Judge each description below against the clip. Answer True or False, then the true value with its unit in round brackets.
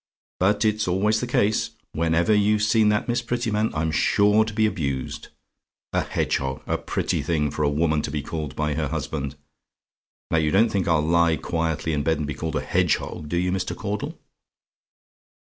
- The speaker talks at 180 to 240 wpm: True (185 wpm)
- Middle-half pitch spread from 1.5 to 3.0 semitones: False (5.5 semitones)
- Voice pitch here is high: False (85 Hz)